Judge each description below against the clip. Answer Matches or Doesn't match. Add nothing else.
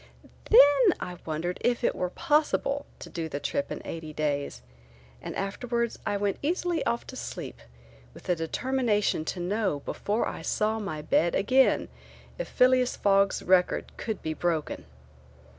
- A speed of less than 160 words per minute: Matches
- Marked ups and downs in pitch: Matches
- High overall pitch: Matches